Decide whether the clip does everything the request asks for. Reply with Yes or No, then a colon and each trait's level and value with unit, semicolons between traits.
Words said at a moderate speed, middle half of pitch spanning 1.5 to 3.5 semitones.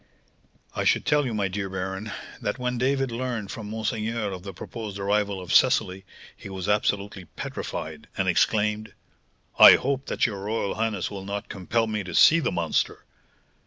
Yes: average, 170 wpm; average, 2.9 semitones